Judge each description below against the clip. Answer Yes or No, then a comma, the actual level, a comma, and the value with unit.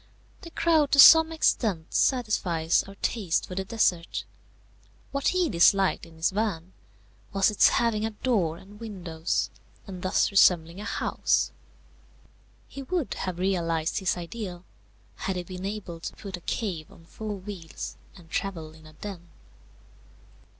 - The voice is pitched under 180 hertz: No, high, 190 Hz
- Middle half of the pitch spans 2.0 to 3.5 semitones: No, average, 4.3 semitones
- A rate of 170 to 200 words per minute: No, average, 150 wpm